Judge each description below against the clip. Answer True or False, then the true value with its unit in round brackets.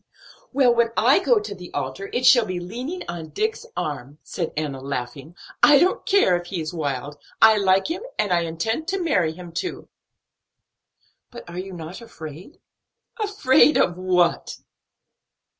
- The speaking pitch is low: False (185 Hz)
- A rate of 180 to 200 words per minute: False (160 wpm)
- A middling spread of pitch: False (7.6 semitones)